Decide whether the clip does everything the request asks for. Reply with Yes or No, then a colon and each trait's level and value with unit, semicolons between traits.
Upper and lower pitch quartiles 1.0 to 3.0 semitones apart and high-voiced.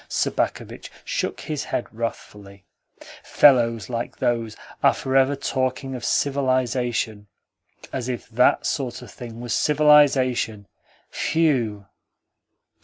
No: average, 2.7 semitones; low, 125 Hz